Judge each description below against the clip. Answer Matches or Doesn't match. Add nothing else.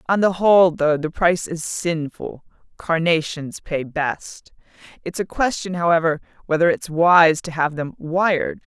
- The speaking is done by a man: Doesn't match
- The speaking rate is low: Doesn't match